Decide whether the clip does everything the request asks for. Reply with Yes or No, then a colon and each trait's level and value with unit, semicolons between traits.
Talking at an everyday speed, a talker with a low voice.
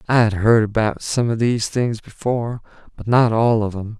No: fast, 210 wpm; low, 115 Hz